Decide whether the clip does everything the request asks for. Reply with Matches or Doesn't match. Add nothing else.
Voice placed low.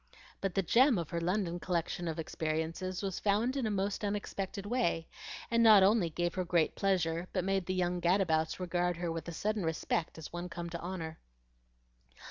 Doesn't match